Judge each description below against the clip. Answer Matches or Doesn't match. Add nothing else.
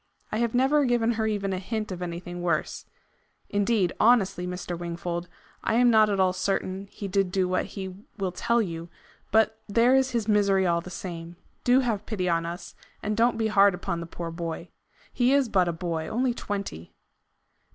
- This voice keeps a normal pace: Matches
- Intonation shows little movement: Doesn't match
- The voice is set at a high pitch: Matches